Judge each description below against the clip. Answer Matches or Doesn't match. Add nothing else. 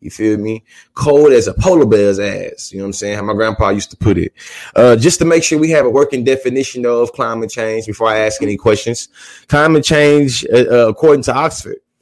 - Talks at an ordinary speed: Doesn't match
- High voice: Doesn't match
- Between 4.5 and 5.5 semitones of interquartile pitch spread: Matches